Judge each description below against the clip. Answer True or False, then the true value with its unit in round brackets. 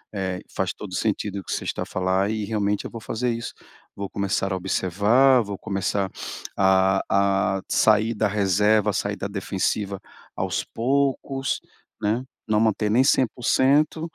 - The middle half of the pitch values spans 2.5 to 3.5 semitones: True (2.8 semitones)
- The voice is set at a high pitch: False (105 Hz)